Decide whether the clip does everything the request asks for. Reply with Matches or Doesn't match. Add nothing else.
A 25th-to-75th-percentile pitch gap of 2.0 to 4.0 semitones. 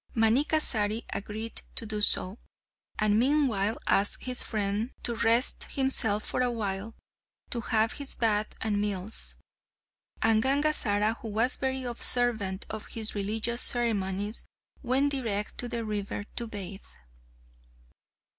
Matches